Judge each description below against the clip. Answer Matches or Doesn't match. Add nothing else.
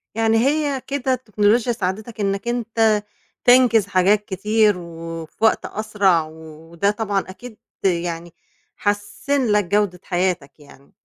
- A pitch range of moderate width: Matches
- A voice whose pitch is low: Doesn't match